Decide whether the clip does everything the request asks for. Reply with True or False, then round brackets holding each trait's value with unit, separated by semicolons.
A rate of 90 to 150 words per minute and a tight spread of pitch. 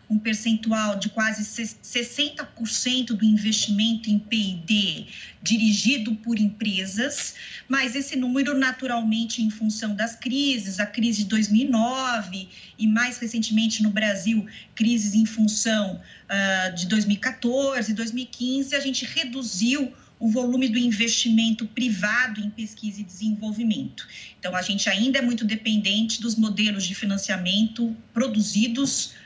True (125 wpm; 2.2 semitones)